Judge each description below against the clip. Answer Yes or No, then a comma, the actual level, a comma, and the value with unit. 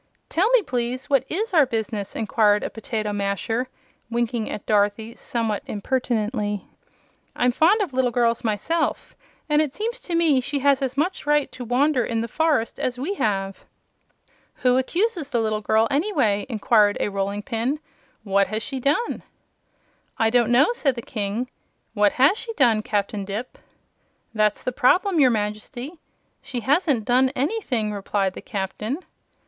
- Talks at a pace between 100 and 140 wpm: No, average, 160 wpm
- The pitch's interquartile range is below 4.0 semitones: No, average, 5.1 semitones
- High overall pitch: Yes, high, 245 Hz